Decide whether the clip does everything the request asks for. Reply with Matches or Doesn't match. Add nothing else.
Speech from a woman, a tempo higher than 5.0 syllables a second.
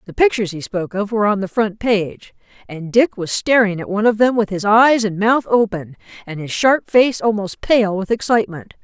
Matches